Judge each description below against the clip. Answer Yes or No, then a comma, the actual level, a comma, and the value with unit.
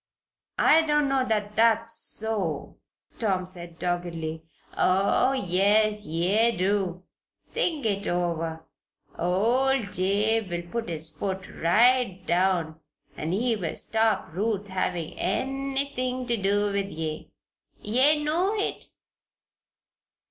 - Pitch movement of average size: Yes, average, 5.0 semitones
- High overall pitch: Yes, high, 205 Hz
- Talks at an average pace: No, slow, 110 wpm